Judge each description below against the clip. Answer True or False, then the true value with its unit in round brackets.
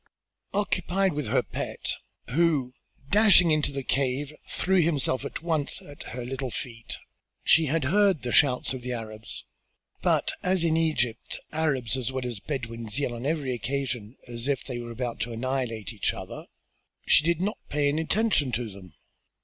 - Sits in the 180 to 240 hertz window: False (135 Hz)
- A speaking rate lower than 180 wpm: True (170 wpm)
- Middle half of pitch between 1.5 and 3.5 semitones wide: False (4.8 semitones)